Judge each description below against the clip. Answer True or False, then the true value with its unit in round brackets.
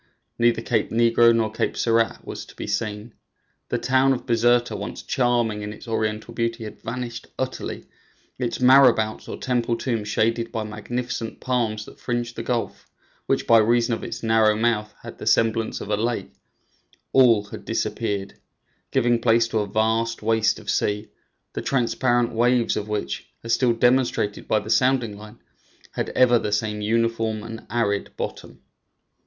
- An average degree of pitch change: False (1.9 semitones)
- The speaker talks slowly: False (165 wpm)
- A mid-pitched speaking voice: False (115 Hz)